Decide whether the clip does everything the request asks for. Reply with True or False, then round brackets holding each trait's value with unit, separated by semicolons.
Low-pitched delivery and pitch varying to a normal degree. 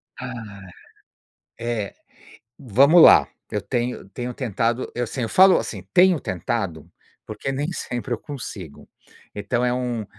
True (120 Hz; 3.6 semitones)